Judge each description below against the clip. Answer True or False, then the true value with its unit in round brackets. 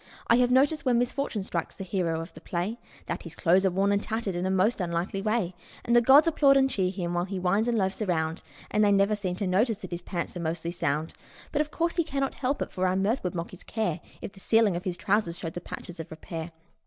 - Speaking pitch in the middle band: False (195 Hz)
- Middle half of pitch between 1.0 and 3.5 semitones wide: False (4.7 semitones)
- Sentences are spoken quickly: True (260 wpm)